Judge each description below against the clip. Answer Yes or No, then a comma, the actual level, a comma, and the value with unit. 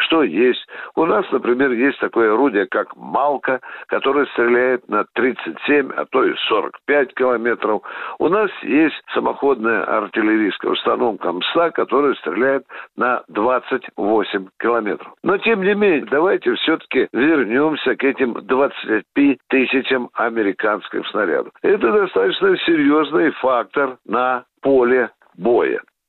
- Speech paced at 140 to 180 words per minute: No, average, 115 wpm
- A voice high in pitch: Yes, very high, 285 Hz